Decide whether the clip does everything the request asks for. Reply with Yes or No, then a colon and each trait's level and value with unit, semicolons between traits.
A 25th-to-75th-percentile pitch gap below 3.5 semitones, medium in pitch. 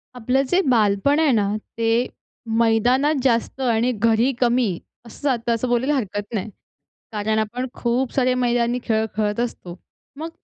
No: narrow, 2.6 semitones; high, 235 Hz